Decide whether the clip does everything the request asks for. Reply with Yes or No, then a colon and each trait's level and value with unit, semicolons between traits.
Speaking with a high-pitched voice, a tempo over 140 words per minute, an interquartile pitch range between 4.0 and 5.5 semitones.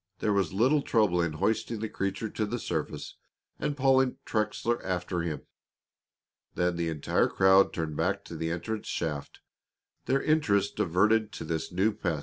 No: low, 100 Hz; average, 160 wpm; average, 4.6 semitones